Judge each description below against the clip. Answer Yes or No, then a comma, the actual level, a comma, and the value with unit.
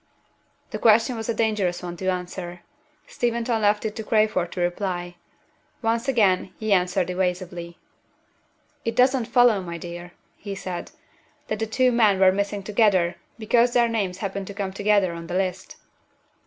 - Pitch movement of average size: Yes, average, 3.7 semitones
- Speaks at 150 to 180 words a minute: Yes, average, 160 wpm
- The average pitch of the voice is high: Yes, high, 200 Hz